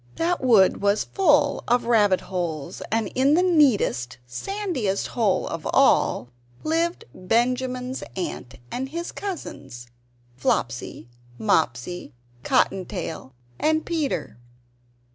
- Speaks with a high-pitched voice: Yes, high, 225 Hz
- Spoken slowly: Yes, slow, 105 wpm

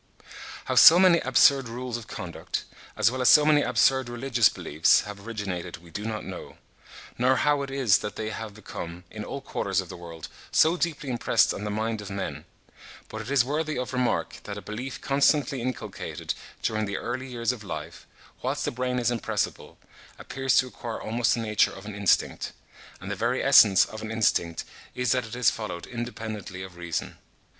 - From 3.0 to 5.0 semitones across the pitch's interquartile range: Yes, average, 3.8 semitones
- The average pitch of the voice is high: No, low, 115 Hz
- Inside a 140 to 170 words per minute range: No, average, 195 wpm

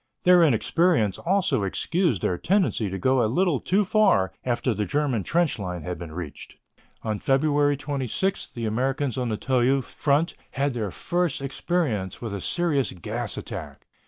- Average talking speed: Yes, average, 160 wpm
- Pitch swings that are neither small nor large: No, wide, 7.0 semitones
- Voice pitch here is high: No, low, 130 Hz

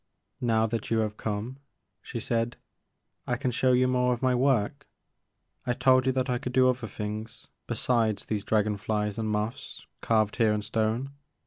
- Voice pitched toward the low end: Yes, low, 115 Hz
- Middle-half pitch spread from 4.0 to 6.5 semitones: No, average, 2.8 semitones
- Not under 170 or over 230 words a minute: Yes, average, 185 wpm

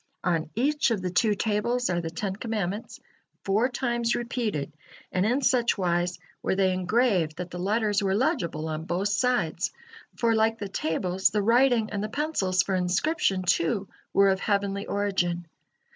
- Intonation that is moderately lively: Yes, average, 4.4 semitones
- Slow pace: No, average, 165 wpm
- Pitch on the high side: Yes, high, 200 Hz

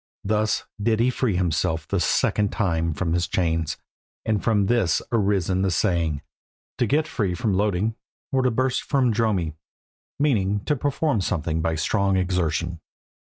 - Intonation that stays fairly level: No, average, 5.1 semitones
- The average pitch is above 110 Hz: No, low, 100 Hz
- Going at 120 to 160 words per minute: Yes, average, 155 wpm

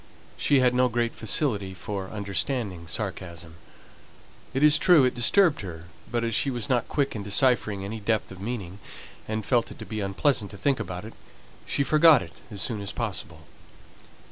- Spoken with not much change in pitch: No, average, 4.6 semitones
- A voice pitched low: Yes, low, 110 Hz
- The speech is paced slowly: No, average, 170 wpm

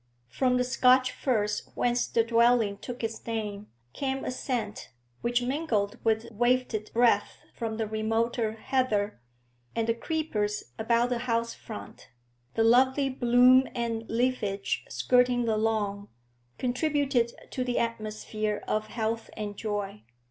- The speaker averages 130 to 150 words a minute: Yes, slow, 135 wpm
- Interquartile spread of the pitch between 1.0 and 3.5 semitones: Yes, narrow, 2.6 semitones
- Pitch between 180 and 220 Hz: No, high, 230 Hz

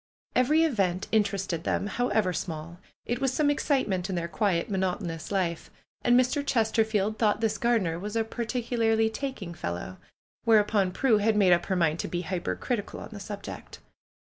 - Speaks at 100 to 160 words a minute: No, average, 170 wpm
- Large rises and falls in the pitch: No, average, 4.3 semitones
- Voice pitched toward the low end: No, high, 210 Hz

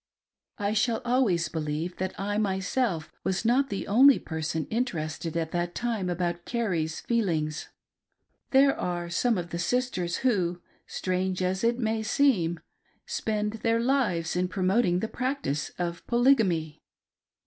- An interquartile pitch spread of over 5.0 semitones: Yes, wide, 5.5 semitones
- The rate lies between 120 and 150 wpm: Yes, average, 145 wpm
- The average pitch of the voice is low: No, high, 190 Hz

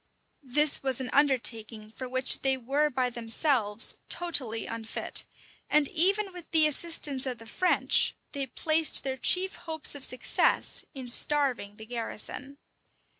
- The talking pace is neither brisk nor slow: Yes, average, 145 wpm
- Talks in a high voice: Yes, very high, 265 Hz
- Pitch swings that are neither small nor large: Yes, average, 4.2 semitones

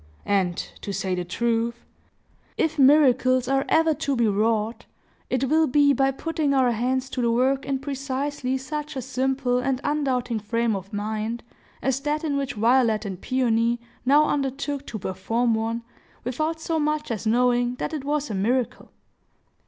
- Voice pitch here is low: No, very high, 255 Hz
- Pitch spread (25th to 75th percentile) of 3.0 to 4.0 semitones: Yes, average, 3.4 semitones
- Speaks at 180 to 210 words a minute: No, average, 165 wpm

